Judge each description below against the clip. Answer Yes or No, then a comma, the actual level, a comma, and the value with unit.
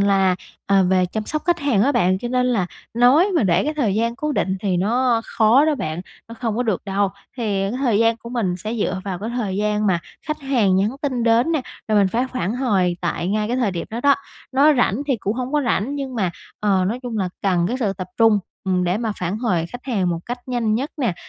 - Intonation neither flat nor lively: Yes, average, 4.5 semitones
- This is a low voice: No, high, 220 Hz